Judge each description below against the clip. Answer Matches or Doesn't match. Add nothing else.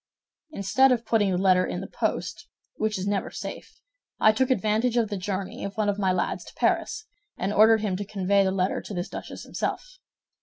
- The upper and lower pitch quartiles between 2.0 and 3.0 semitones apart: Matches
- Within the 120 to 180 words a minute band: Doesn't match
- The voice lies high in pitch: Matches